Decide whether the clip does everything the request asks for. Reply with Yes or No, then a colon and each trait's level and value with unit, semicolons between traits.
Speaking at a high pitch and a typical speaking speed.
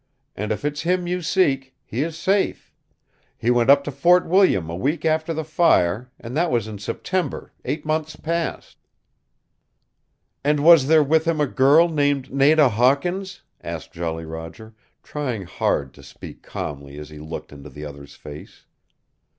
No: medium, 140 Hz; average, 165 wpm